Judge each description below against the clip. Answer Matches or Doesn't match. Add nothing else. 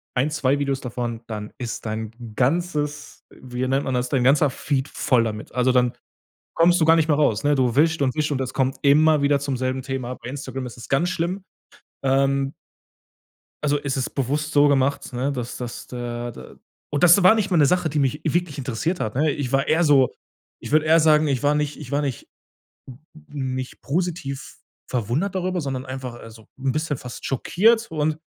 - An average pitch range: Matches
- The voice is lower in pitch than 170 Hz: Matches